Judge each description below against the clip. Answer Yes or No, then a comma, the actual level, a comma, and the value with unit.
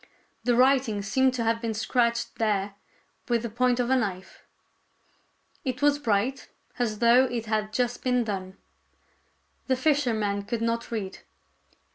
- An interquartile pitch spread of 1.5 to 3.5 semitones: Yes, average, 2.9 semitones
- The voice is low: No, high, 235 Hz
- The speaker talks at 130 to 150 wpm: Yes, average, 145 wpm